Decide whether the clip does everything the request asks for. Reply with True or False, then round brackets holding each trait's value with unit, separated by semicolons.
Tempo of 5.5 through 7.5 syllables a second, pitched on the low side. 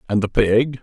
False (4.6 syllables/s; 115 Hz)